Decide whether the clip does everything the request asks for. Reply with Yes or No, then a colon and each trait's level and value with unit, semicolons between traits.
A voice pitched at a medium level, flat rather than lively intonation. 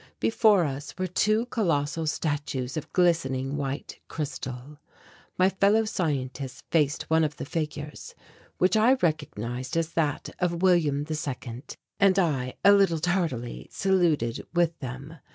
No: medium, 155 Hz; average, 4.7 semitones